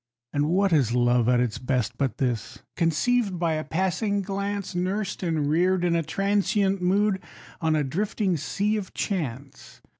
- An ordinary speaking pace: Yes, average, 160 wpm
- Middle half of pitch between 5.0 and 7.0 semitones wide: Yes, wide, 5.4 semitones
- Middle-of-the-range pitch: Yes, medium, 175 Hz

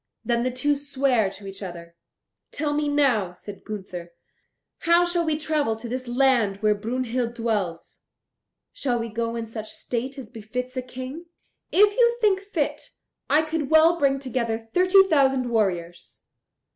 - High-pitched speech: Yes, very high, 250 Hz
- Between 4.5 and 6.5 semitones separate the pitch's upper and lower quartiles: Yes, average, 5.0 semitones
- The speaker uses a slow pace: No, average, 160 wpm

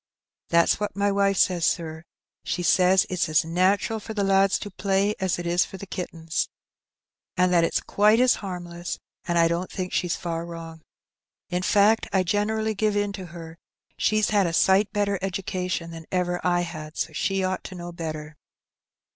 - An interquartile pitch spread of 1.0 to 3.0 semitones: Yes, average, 2.7 semitones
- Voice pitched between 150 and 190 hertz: Yes, medium, 185 Hz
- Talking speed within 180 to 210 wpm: Yes, average, 190 wpm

